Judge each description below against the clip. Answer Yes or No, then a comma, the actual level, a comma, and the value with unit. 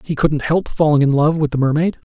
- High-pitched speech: No, medium, 150 Hz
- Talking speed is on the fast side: Yes, fast, 255 wpm